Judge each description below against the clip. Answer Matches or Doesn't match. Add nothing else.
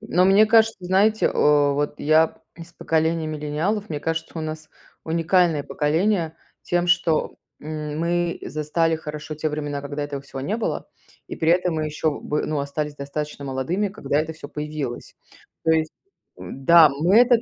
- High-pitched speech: Doesn't match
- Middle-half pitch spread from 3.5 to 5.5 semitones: Doesn't match